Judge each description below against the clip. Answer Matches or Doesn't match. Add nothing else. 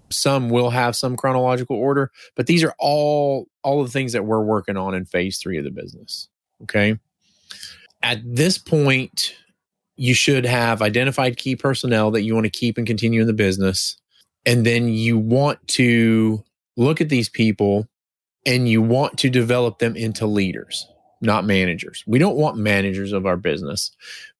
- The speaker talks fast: Doesn't match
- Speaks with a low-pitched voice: Matches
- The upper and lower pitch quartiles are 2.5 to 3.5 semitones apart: Matches